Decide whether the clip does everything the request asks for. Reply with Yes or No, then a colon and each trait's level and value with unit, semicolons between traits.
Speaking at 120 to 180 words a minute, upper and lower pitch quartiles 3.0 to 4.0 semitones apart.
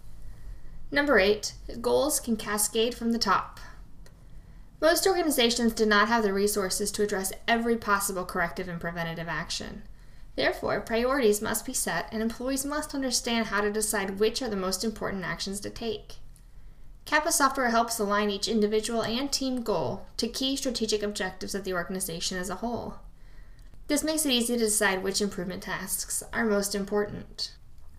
Yes: average, 160 wpm; average, 3.3 semitones